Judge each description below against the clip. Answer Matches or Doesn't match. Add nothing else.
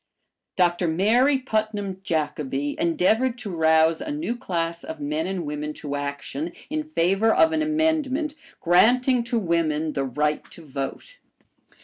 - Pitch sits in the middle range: Matches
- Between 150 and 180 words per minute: Doesn't match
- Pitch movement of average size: Doesn't match